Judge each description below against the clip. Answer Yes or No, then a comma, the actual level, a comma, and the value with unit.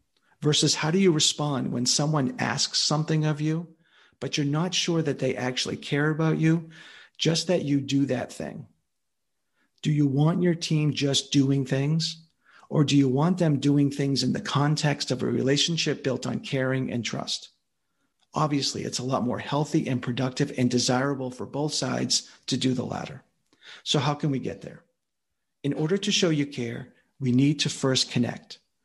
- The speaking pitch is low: No, medium, 145 Hz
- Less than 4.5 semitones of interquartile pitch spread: Yes, average, 3.0 semitones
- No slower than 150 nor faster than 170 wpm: No, average, 180 wpm